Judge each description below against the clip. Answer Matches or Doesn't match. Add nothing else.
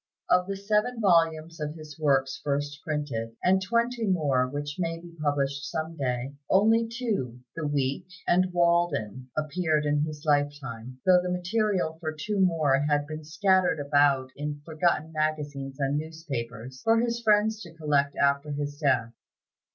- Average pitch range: Matches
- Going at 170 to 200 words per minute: Doesn't match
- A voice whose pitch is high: Doesn't match